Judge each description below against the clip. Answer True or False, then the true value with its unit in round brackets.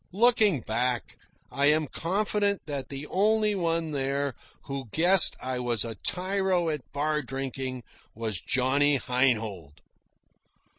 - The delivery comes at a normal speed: False (120 wpm)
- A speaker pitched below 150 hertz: True (140 Hz)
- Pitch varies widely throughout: True (5.9 semitones)